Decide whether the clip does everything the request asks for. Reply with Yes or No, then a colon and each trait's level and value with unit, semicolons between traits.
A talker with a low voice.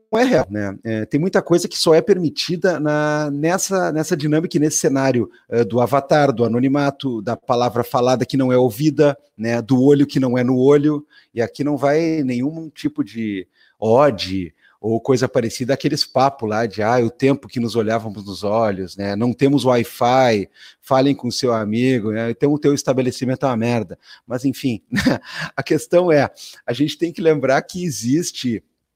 Yes: low, 130 Hz